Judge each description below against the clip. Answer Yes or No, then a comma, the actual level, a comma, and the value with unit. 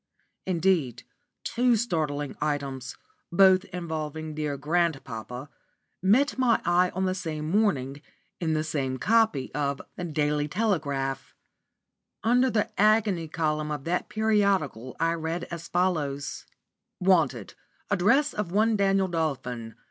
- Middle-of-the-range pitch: Yes, medium, 165 Hz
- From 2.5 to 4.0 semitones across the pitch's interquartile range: No, average, 5.1 semitones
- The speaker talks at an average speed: No, slow, 120 wpm